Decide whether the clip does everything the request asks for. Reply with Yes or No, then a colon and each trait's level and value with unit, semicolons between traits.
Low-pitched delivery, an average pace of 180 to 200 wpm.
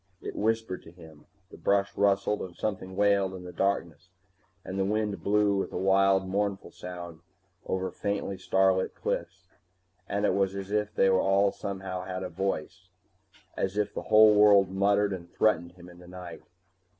No: very low, 95 Hz; average, 165 wpm